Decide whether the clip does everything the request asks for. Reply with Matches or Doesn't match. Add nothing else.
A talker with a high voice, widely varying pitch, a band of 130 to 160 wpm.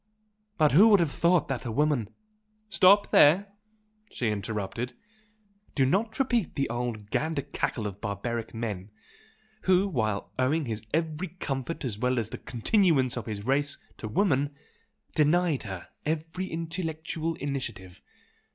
Doesn't match